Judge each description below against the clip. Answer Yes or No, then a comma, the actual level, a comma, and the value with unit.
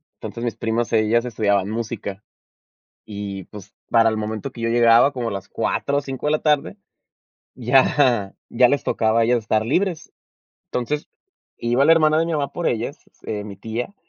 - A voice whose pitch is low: Yes, low, 115 Hz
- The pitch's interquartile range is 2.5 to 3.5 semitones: No, average, 4.3 semitones